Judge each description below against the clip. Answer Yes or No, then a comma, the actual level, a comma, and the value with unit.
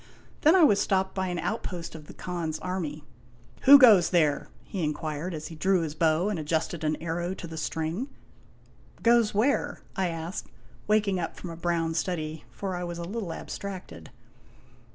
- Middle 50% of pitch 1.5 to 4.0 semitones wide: Yes, average, 3.3 semitones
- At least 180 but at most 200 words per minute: Yes, average, 190 wpm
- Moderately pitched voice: Yes, medium, 175 Hz